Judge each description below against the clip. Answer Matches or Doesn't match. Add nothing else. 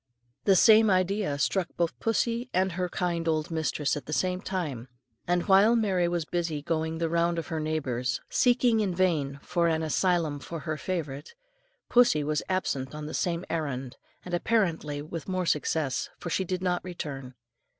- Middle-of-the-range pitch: Matches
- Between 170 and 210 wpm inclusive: Matches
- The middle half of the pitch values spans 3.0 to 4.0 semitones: Matches